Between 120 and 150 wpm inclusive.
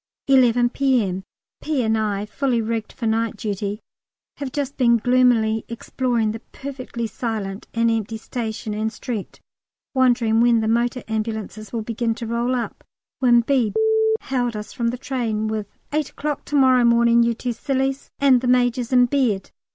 No: average, 165 wpm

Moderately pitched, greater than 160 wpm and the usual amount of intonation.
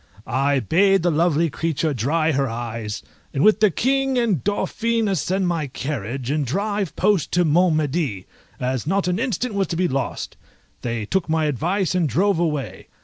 No: medium, 165 Hz; average, 175 wpm; wide, 6.0 semitones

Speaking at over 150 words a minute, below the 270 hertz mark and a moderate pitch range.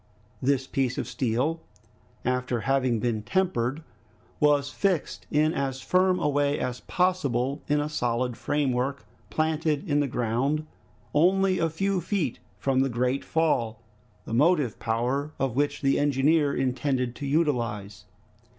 No: average, 140 wpm; medium, 140 Hz; average, 3.6 semitones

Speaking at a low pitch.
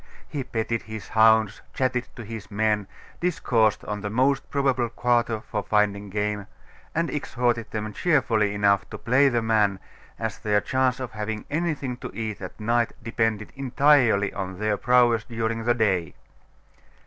Yes: low, 110 Hz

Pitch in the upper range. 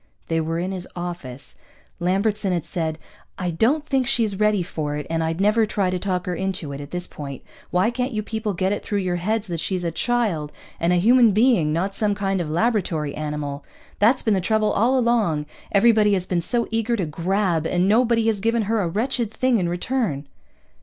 Yes: high, 195 Hz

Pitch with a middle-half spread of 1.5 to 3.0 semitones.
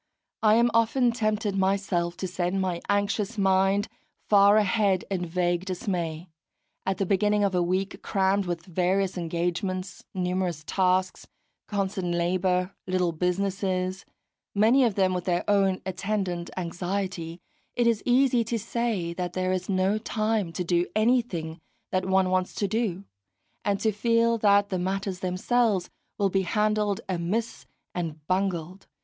Yes: narrow, 2.4 semitones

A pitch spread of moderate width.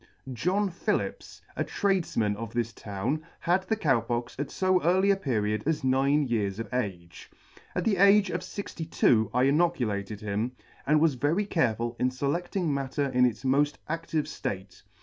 No: wide, 6.9 semitones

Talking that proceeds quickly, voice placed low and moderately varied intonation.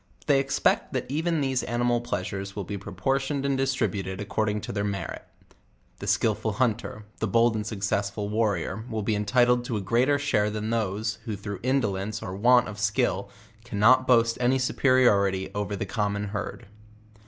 No: average, 180 wpm; low, 110 Hz; average, 3.5 semitones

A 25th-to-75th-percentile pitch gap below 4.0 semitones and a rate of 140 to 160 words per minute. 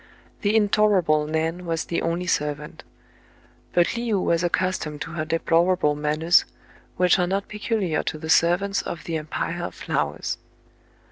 Yes: average, 2.9 semitones; average, 155 wpm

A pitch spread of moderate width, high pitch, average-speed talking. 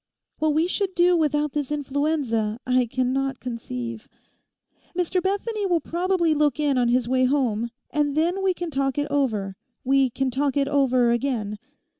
Yes: average, 4.0 semitones; very high, 275 Hz; average, 160 wpm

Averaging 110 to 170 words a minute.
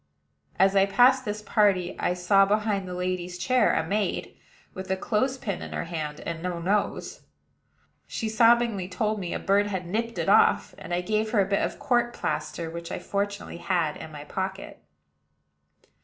No: average, 185 wpm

